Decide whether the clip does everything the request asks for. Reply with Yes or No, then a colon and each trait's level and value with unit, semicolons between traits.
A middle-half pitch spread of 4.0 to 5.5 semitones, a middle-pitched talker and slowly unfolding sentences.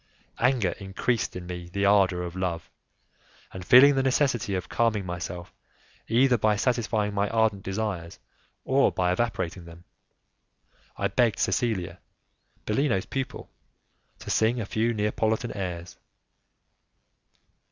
No: average, 4.4 semitones; low, 105 Hz; slow, 120 wpm